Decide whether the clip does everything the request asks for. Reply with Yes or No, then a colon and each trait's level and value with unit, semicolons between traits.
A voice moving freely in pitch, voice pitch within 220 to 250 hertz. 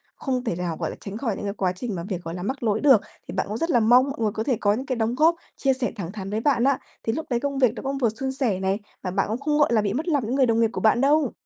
No: average, 4.8 semitones; high, 235 Hz